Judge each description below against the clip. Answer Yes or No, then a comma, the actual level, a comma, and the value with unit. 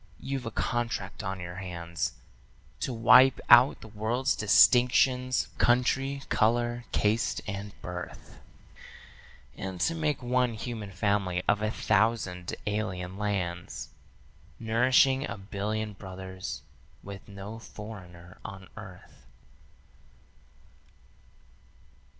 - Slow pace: Yes, slow, 100 wpm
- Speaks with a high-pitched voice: No, low, 110 Hz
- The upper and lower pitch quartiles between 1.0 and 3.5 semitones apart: No, average, 4.1 semitones